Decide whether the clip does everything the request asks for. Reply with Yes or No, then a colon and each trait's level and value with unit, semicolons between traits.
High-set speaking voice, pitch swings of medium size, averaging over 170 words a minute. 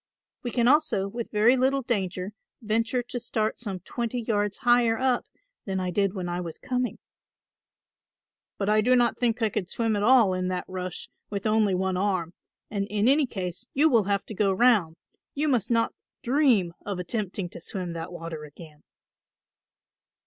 Yes: high, 210 Hz; average, 4.5 semitones; average, 180 wpm